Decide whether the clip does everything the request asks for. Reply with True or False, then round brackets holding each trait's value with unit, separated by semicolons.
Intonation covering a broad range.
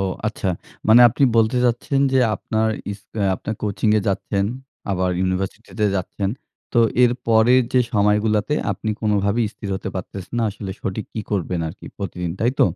False (2.5 semitones)